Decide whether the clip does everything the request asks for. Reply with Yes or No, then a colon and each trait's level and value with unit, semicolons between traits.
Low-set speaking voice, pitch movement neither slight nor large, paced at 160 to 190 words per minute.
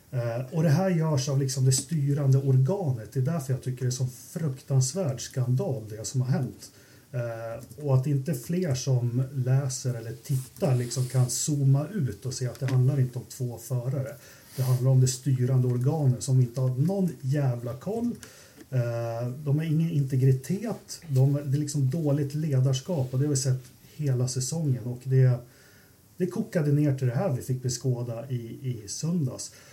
No: low, 130 Hz; narrow, 2.2 semitones; average, 180 wpm